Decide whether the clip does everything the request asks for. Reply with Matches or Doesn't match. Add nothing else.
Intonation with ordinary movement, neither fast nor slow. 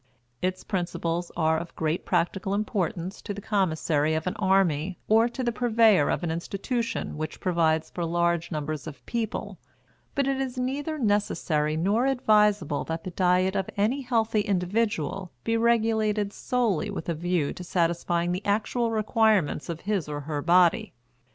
Matches